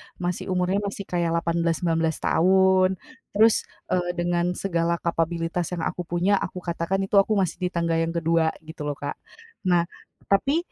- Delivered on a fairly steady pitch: Yes, narrow, 2.0 semitones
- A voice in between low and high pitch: Yes, medium, 175 Hz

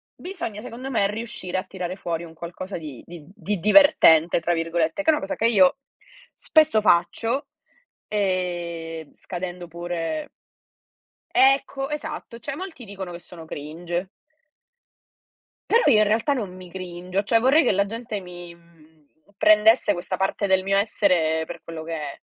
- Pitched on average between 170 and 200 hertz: Yes, medium, 185 Hz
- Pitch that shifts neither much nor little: Yes, average, 4.4 semitones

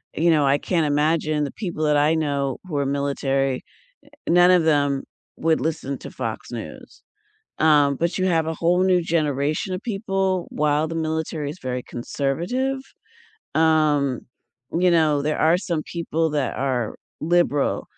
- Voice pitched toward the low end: No, medium, 155 Hz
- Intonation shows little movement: No, average, 3.0 semitones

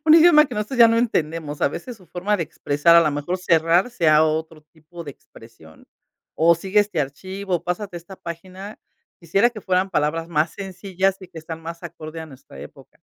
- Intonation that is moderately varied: Yes, average, 3.7 semitones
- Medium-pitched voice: Yes, medium, 170 Hz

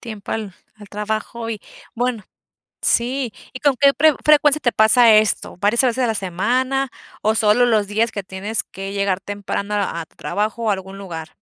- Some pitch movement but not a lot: Yes, average, 3.4 semitones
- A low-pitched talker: No, high, 215 Hz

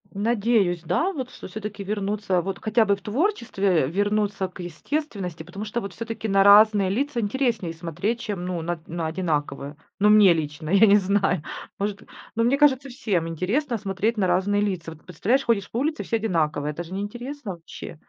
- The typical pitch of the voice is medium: No, high, 200 Hz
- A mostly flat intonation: No, average, 4.3 semitones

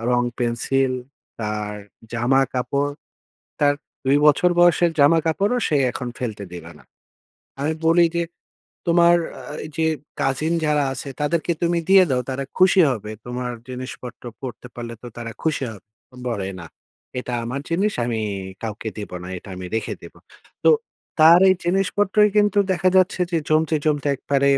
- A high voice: No, medium, 140 Hz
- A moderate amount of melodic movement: No, wide, 5.8 semitones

